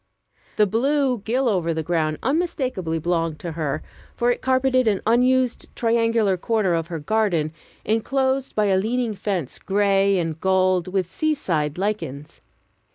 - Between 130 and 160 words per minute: Yes, average, 150 wpm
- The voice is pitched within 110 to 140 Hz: No, high, 200 Hz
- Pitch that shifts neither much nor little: No, wide, 6.3 semitones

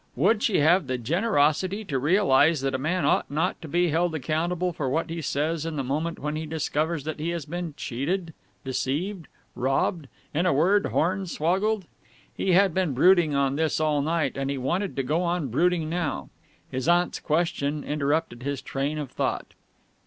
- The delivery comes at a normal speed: Yes, average, 180 wpm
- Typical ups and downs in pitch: Yes, average, 3.7 semitones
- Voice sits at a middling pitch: Yes, medium, 160 Hz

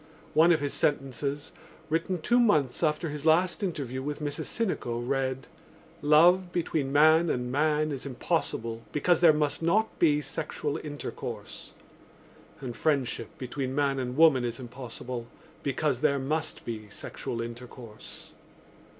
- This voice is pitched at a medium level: Yes, medium, 145 Hz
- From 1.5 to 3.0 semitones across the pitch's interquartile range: No, average, 3.7 semitones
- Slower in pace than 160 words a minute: Yes, slow, 135 wpm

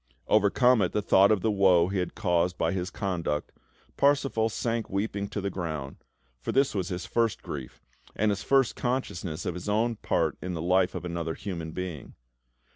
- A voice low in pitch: Yes, very low, 95 Hz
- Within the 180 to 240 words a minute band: Yes, average, 190 wpm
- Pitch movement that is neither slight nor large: Yes, average, 3.7 semitones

